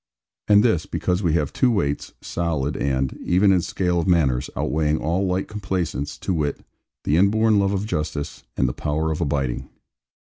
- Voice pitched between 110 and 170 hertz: No, very low, 85 Hz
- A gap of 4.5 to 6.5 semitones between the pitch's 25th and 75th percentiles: Yes, average, 4.8 semitones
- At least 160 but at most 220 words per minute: Yes, average, 175 wpm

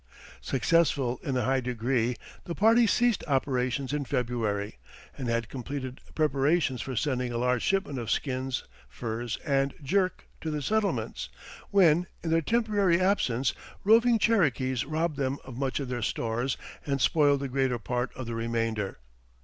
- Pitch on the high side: No, low, 135 Hz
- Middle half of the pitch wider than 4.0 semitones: Yes, average, 4.8 semitones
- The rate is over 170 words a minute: No, average, 155 wpm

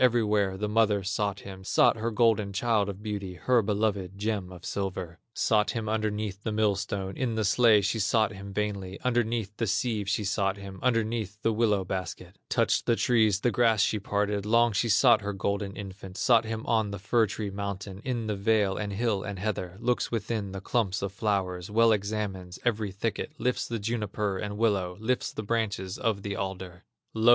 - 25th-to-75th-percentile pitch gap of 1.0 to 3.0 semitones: Yes, narrow, 2.4 semitones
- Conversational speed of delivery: Yes, average, 190 wpm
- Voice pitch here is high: No, low, 105 Hz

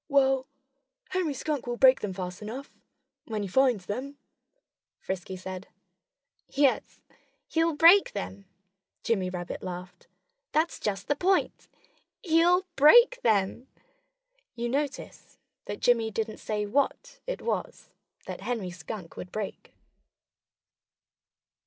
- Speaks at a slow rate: Yes, slow, 115 wpm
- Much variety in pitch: Yes, wide, 7.0 semitones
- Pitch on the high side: Yes, high, 240 Hz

